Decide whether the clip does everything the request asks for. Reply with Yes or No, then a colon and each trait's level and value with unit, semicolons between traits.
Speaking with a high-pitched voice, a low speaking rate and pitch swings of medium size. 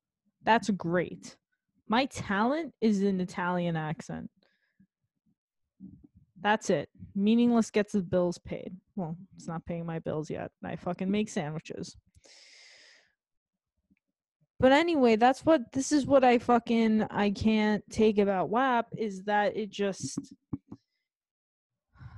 Yes: high, 205 Hz; slow, 120 wpm; average, 4.4 semitones